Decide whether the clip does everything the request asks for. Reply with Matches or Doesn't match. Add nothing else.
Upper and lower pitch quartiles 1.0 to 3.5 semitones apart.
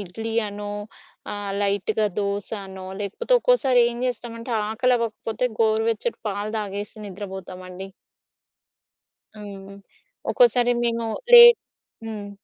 Matches